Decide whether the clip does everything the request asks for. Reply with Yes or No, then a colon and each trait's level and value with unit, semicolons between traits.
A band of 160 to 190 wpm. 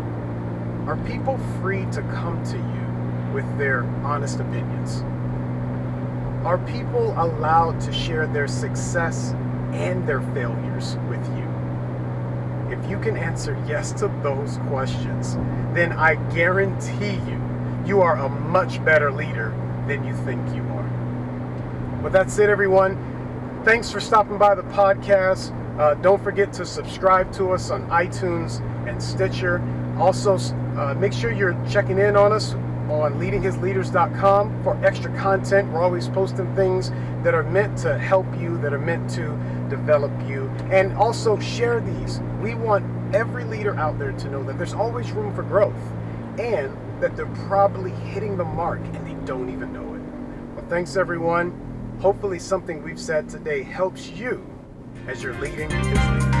No: average, 150 wpm